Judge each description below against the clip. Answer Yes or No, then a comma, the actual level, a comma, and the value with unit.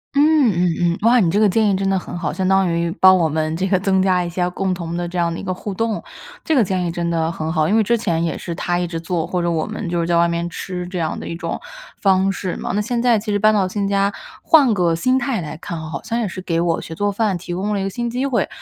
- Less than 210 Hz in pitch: Yes, medium, 185 Hz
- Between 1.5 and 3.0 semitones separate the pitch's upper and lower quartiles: No, average, 3.4 semitones